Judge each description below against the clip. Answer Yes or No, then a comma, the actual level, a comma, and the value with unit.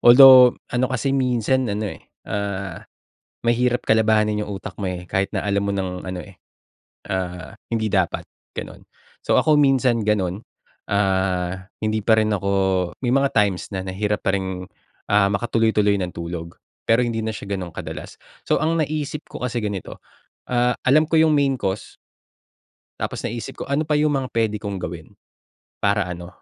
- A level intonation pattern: No, average, 4.4 semitones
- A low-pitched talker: Yes, low, 105 Hz